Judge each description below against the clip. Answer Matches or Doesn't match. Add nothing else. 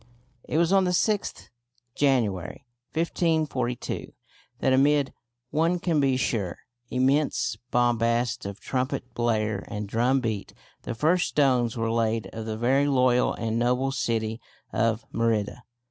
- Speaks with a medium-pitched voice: Doesn't match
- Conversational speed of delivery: Doesn't match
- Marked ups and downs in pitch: Doesn't match